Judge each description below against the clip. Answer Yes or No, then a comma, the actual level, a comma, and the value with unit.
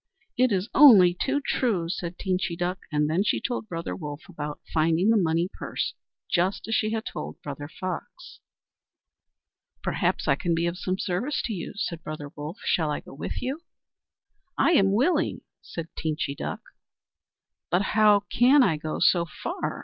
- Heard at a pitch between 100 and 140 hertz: No, medium, 180 Hz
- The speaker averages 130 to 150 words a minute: No, average, 170 wpm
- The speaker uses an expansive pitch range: No, average, 5.0 semitones